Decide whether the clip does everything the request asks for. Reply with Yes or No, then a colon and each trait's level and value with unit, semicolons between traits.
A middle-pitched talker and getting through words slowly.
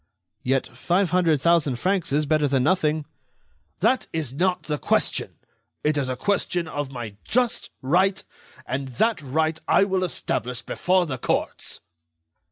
No: medium, 160 Hz; average, 150 wpm